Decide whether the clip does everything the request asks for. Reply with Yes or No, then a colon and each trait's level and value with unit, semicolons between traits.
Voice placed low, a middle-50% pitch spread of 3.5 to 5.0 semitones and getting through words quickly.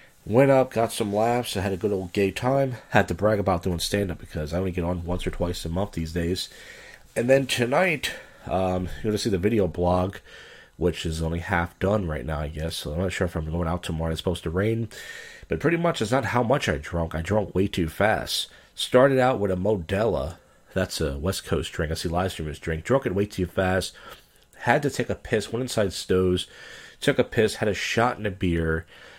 Yes: very low, 95 Hz; average, 4.2 semitones; fast, 235 wpm